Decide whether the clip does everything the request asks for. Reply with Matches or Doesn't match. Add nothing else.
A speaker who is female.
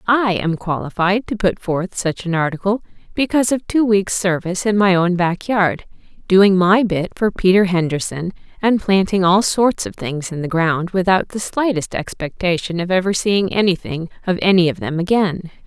Matches